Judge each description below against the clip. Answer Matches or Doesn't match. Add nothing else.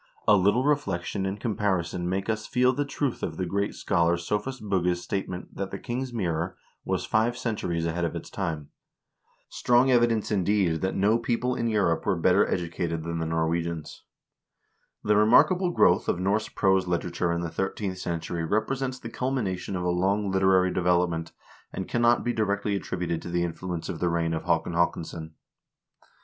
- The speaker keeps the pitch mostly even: Doesn't match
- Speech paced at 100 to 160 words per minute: Doesn't match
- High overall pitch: Doesn't match